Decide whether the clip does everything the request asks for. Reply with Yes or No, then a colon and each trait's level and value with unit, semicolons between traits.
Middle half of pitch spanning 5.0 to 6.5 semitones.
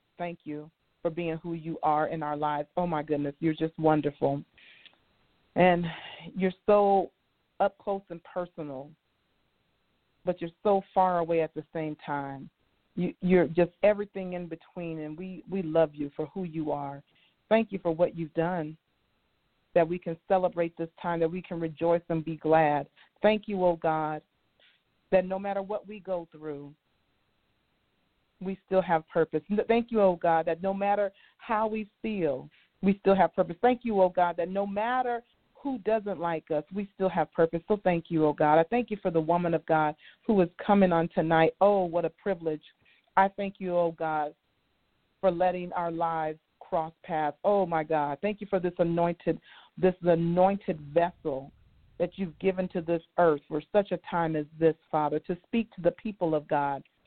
No: average, 3.3 semitones